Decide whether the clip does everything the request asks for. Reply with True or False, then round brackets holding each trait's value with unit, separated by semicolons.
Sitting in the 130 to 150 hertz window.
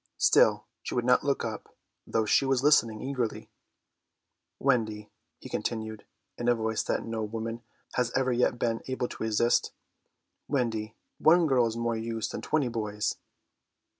False (115 Hz)